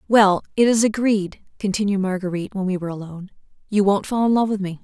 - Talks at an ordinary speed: No, fast, 210 wpm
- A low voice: No, high, 200 Hz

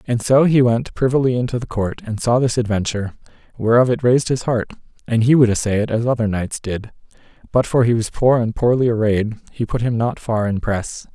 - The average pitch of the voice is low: Yes, low, 115 Hz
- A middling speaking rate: No, fast, 220 wpm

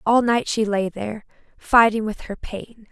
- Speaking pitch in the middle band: No, high, 220 Hz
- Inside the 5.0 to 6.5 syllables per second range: No, 4.4 syllables/s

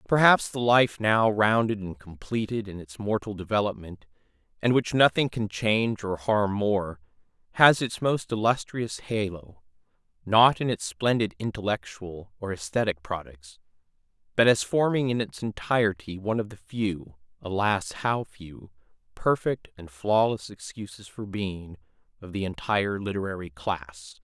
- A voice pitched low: Yes, low, 105 Hz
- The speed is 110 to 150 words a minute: Yes, average, 140 wpm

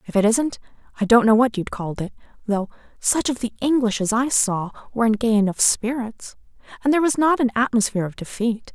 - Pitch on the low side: No, high, 230 Hz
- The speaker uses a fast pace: Yes, fast, 215 wpm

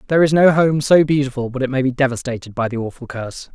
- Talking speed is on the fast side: Yes, fast, 255 wpm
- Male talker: Yes, male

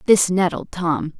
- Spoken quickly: No, average, 150 wpm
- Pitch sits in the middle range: Yes, medium, 170 Hz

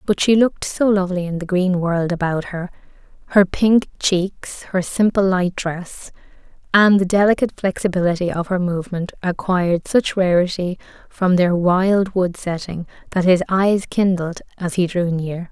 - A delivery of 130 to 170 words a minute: Yes, average, 160 wpm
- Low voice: No, medium, 185 Hz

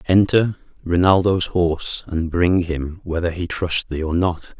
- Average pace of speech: Yes, average, 155 wpm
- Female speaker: No, male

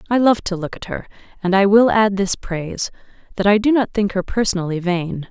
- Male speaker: No, female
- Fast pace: Yes, fast, 225 wpm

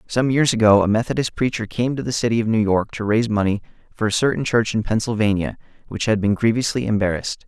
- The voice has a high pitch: No, low, 110 Hz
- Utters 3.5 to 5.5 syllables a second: No, 6.4 syllables/s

